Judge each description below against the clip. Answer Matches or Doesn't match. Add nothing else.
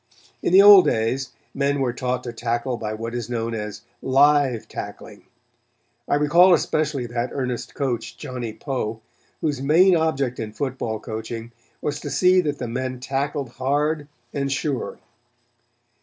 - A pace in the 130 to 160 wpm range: Matches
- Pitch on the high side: Doesn't match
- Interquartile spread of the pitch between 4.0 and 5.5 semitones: Doesn't match